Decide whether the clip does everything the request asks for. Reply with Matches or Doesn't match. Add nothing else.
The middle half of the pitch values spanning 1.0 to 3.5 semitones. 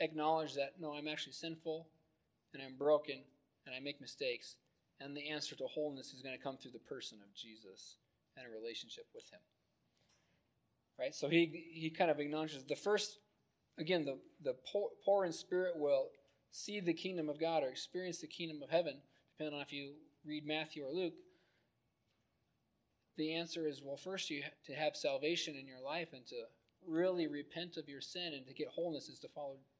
Matches